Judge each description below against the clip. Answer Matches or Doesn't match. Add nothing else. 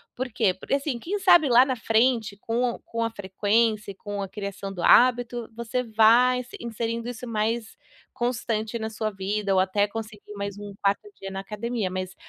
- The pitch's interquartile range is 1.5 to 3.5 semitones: Matches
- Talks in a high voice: Matches